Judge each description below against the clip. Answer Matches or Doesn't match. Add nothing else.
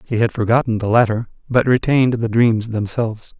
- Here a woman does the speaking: Doesn't match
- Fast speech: Doesn't match